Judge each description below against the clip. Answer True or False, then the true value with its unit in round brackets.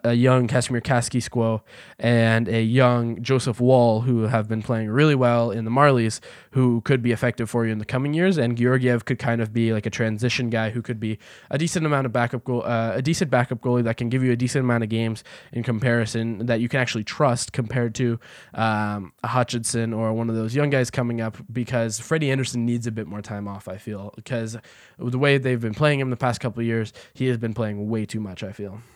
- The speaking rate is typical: False (235 wpm)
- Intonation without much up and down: True (2.0 semitones)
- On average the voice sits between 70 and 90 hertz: False (120 Hz)